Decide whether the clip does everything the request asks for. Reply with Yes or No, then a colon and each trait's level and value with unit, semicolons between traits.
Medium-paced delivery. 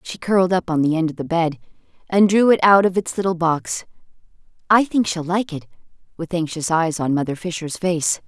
No: fast, 210 wpm